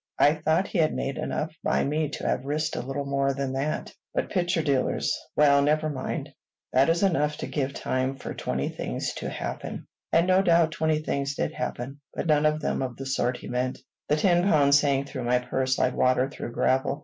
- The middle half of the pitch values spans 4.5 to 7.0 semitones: No, average, 2.7 semitones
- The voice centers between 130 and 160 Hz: Yes, medium, 140 Hz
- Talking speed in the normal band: No, fast, 210 wpm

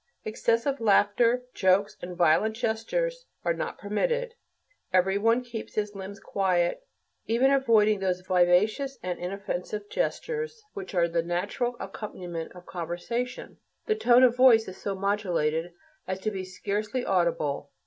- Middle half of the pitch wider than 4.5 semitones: Yes, average, 5.0 semitones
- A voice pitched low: No, high, 205 Hz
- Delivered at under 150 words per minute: Yes, average, 140 wpm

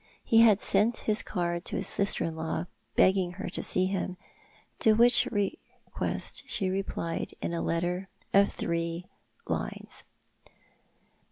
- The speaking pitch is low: No, medium, 185 Hz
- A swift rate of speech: No, slow, 135 wpm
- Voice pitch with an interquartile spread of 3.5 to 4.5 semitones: No, average, 2.7 semitones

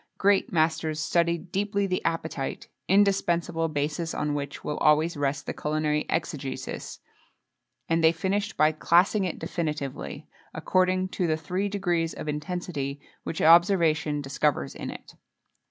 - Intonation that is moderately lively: Yes, average, 3.3 semitones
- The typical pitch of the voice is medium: Yes, medium, 165 Hz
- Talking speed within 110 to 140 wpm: Yes, slow, 135 wpm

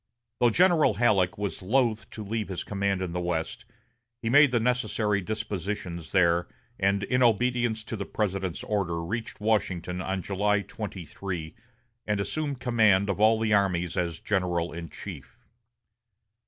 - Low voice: Yes, low, 100 Hz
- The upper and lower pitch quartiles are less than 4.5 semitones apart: Yes, average, 3.7 semitones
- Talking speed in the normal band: Yes, average, 150 wpm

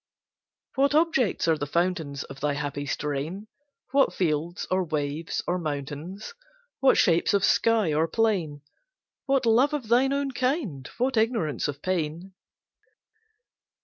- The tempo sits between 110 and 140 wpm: Yes, slow, 135 wpm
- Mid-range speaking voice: Yes, medium, 180 Hz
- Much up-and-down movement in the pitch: Yes, wide, 7.9 semitones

